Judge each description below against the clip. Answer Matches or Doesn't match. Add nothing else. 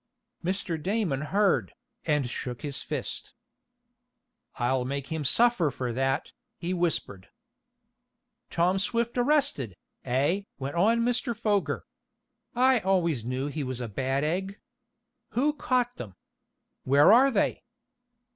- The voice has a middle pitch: Matches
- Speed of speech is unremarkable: Doesn't match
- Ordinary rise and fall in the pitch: Doesn't match